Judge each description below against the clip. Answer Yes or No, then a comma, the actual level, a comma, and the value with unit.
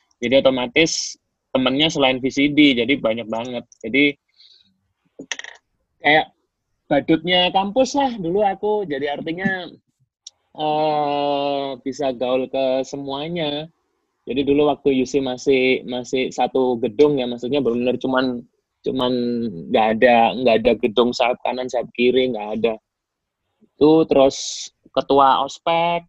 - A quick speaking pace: No, average, 120 wpm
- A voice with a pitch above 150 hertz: No, low, 135 Hz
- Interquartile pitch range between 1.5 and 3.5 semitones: Yes, average, 3.0 semitones